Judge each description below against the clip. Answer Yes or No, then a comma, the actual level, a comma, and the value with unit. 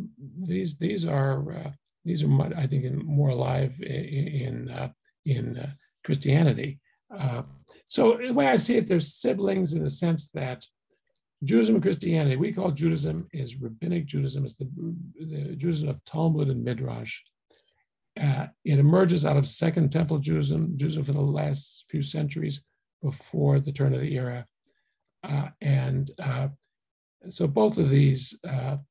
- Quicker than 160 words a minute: No, average, 155 wpm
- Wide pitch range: No, average, 3.2 semitones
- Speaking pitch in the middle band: Yes, medium, 145 Hz